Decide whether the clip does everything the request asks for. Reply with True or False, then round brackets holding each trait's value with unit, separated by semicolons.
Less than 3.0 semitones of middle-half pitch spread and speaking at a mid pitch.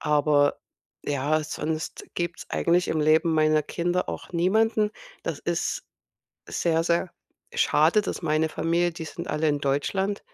True (2.4 semitones; 160 Hz)